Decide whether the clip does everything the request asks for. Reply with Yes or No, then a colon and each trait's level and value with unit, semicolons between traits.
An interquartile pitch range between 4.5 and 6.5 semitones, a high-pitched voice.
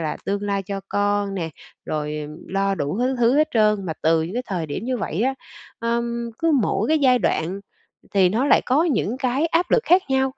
Yes: wide, 5.4 semitones; high, 210 Hz